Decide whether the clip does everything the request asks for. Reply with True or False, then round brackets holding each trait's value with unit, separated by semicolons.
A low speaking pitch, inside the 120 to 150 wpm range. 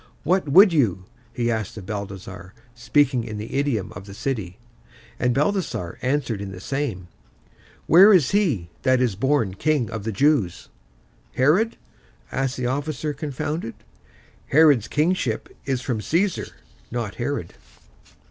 True (125 Hz; 140 wpm)